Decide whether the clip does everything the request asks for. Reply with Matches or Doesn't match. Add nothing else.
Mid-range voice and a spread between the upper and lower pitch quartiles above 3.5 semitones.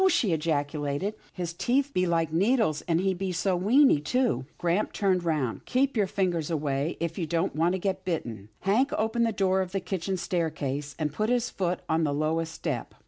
Matches